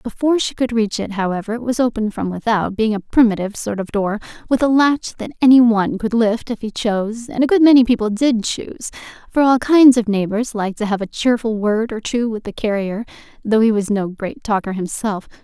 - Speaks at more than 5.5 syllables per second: Yes, 5.7 syllables/s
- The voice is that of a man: No, female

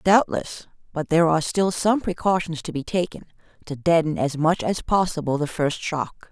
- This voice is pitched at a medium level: Yes, medium, 165 Hz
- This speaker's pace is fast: No, average, 180 wpm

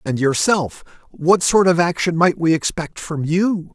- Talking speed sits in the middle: Yes, average, 160 wpm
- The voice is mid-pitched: Yes, medium, 170 Hz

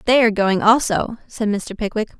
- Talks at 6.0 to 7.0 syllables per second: No, 5.4 syllables/s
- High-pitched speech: Yes, high, 215 Hz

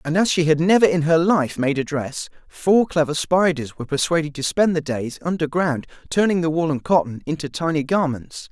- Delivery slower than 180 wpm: No, fast, 205 wpm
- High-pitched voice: No, medium, 160 Hz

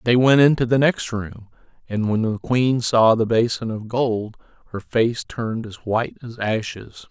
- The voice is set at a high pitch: No, low, 115 Hz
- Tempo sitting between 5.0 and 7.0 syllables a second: No, 4.4 syllables/s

